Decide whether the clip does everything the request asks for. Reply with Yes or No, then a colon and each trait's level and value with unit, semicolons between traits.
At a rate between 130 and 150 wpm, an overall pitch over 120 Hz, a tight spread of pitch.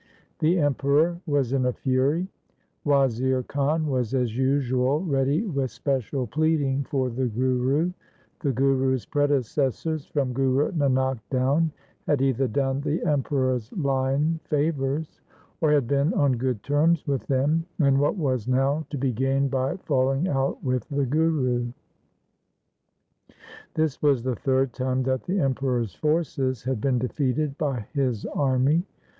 Yes: average, 140 wpm; low, 135 Hz; narrow, 2.2 semitones